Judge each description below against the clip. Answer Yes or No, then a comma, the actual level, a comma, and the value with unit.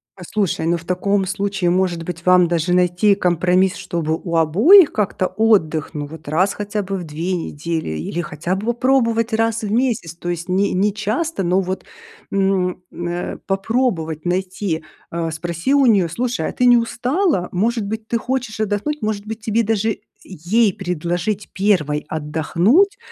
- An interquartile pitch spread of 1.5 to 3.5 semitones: No, average, 4.3 semitones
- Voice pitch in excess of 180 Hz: Yes, high, 190 Hz